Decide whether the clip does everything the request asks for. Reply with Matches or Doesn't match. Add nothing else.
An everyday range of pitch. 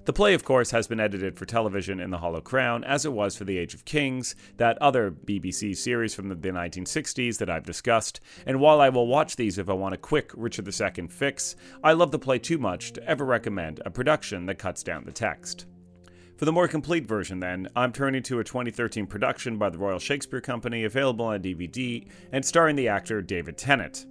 Doesn't match